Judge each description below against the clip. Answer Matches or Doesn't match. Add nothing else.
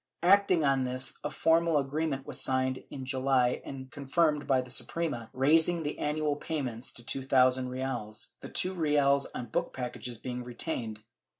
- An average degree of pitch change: Matches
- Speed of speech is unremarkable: Matches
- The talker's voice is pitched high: Doesn't match